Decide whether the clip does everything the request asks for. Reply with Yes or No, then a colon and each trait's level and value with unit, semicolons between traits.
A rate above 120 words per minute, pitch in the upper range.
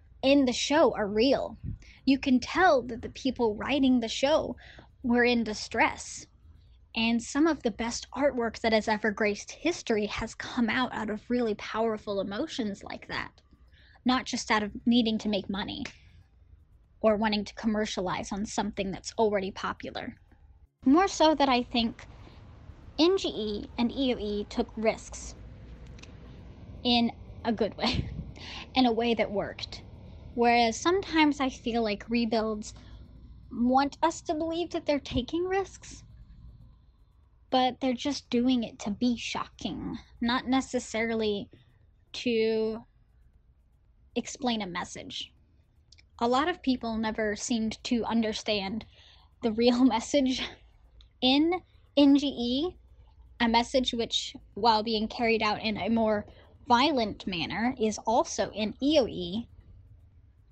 Yes: average, 130 wpm; high, 230 Hz